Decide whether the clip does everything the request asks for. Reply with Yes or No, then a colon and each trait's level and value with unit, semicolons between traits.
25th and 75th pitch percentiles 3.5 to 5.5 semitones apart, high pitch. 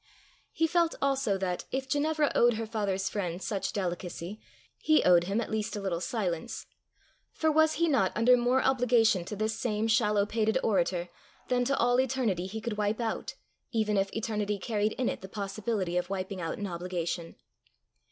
Yes: average, 4.3 semitones; high, 215 Hz